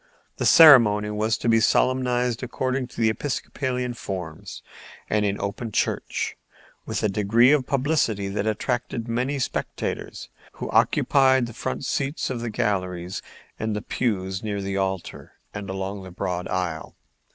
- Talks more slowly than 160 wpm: Yes, average, 150 wpm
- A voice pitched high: No, low, 110 Hz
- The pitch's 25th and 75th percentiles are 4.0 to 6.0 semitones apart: Yes, average, 4.3 semitones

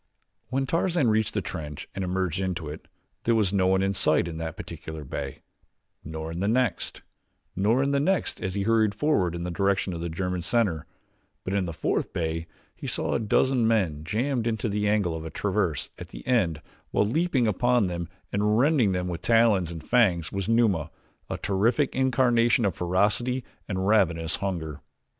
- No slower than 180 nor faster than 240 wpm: Yes, average, 185 wpm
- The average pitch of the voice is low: Yes, low, 100 Hz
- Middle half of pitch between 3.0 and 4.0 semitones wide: No, average, 5.2 semitones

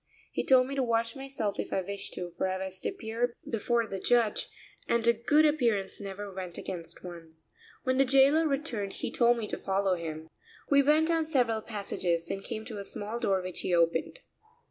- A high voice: Yes, high, 220 Hz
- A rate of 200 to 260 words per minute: Yes, fast, 205 wpm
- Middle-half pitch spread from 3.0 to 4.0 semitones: No, average, 5.3 semitones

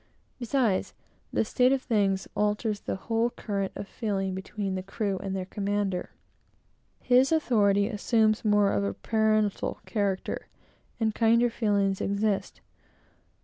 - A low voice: No, high, 210 Hz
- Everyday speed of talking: No, slow, 130 wpm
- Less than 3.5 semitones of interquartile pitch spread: Yes, narrow, 2.4 semitones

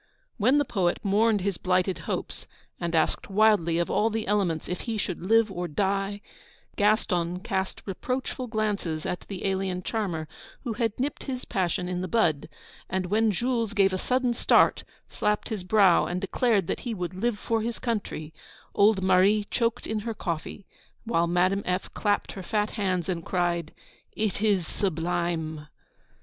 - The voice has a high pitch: Yes, high, 195 Hz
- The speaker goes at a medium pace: Yes, average, 165 wpm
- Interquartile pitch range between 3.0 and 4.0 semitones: Yes, average, 3.6 semitones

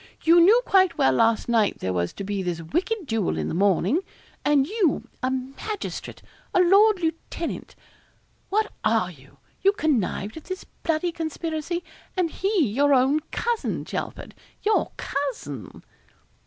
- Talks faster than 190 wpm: No, average, 145 wpm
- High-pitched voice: Yes, very high, 295 Hz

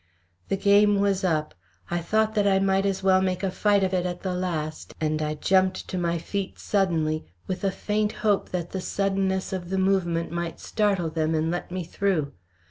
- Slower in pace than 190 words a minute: No, fast, 205 wpm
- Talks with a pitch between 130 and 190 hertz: Yes, medium, 185 Hz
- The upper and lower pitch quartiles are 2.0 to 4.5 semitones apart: Yes, narrow, 2.5 semitones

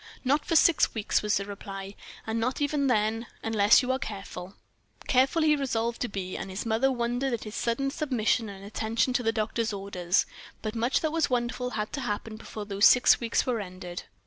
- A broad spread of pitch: No, average, 3.7 semitones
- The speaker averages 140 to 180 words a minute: No, average, 200 wpm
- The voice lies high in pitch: Yes, high, 225 Hz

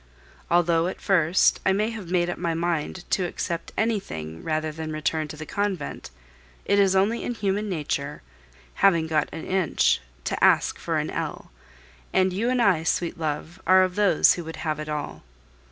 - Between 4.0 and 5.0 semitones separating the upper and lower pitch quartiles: No, average, 3.6 semitones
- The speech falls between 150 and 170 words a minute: No, average, 185 wpm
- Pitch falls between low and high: Yes, medium, 175 Hz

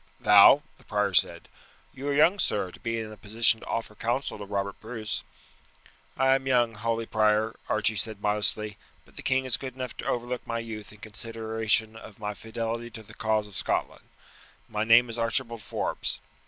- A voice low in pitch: Yes, low, 115 Hz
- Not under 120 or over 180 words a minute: No, average, 190 wpm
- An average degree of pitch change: No, narrow, 1.9 semitones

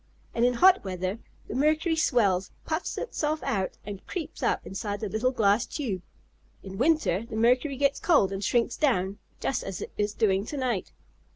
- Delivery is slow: No, average, 180 wpm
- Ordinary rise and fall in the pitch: No, wide, 6.5 semitones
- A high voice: Yes, high, 230 Hz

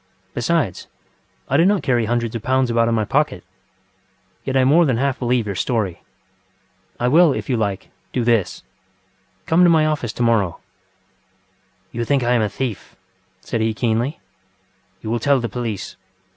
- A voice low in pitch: Yes, low, 120 Hz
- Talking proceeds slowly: No, average, 175 wpm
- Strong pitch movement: No, average, 3.1 semitones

